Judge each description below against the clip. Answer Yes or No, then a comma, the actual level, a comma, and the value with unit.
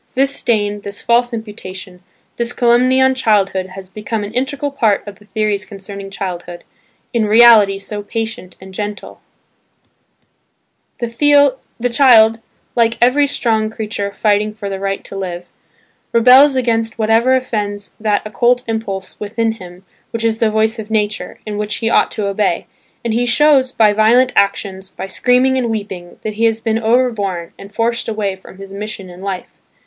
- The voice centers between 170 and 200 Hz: No, high, 215 Hz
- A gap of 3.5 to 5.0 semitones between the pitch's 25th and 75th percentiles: No, average, 2.9 semitones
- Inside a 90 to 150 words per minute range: No, average, 165 wpm